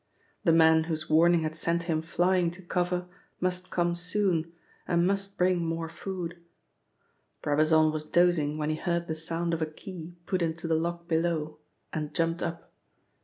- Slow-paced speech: No, average, 170 wpm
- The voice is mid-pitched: Yes, medium, 170 Hz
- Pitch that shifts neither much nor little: No, narrow, 1.6 semitones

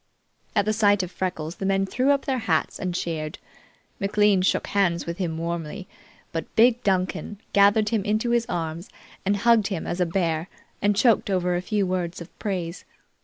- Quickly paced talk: No, average, 185 wpm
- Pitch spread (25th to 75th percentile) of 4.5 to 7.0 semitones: No, average, 3.5 semitones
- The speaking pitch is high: Yes, high, 195 Hz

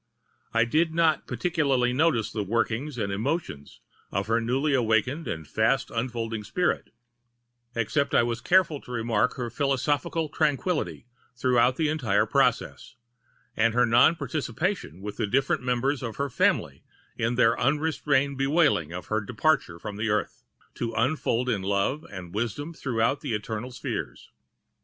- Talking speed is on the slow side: No, average, 145 wpm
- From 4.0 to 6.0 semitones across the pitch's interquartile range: Yes, average, 4.7 semitones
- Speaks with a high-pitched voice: No, low, 125 Hz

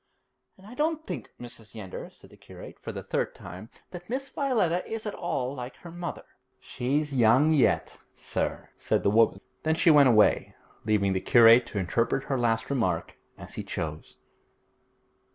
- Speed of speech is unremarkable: Yes, average, 170 wpm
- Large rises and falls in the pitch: Yes, wide, 7.6 semitones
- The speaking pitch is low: Yes, low, 130 Hz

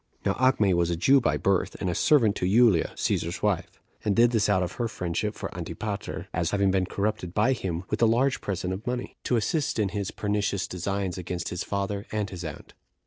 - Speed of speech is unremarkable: No, fast, 215 wpm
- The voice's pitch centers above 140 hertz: No, low, 100 Hz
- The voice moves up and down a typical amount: Yes, average, 3.3 semitones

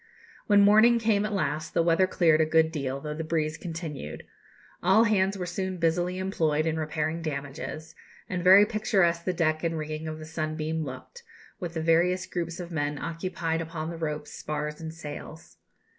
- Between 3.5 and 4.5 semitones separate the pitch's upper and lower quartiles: No, average, 2.7 semitones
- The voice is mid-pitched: Yes, medium, 165 Hz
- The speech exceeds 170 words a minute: Yes, average, 180 wpm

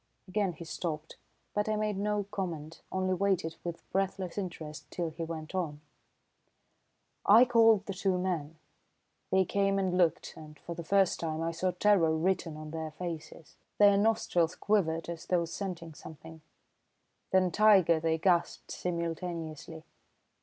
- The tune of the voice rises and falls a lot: No, average, 3.2 semitones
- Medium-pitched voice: Yes, medium, 175 Hz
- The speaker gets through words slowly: No, average, 145 wpm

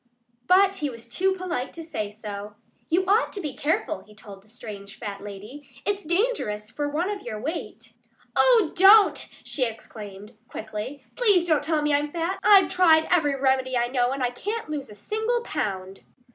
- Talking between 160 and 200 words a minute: Yes, average, 185 wpm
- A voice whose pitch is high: Yes, very high, 290 Hz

